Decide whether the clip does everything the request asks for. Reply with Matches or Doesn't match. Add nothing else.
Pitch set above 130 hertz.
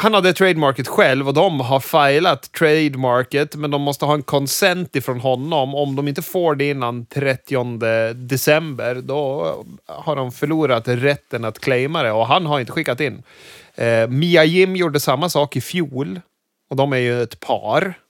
Matches